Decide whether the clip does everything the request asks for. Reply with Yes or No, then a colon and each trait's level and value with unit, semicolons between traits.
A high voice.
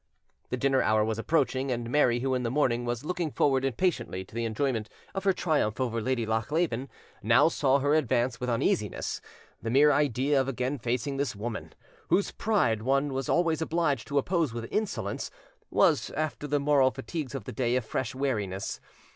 No: low, 130 Hz